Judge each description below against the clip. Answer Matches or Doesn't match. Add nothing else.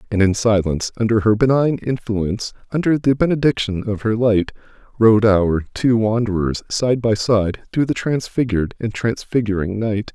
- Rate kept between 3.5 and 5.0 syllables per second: Matches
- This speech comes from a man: Matches